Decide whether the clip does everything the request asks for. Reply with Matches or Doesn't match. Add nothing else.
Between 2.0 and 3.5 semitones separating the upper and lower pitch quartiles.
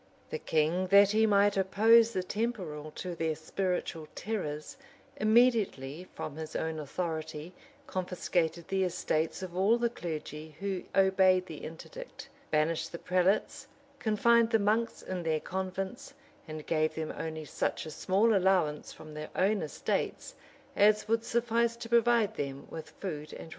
Doesn't match